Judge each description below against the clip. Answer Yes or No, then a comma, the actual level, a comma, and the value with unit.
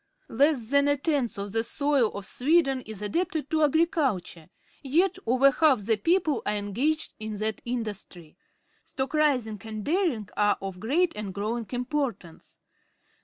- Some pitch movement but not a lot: No, wide, 6.0 semitones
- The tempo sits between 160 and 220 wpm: No, average, 150 wpm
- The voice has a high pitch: Yes, very high, 250 Hz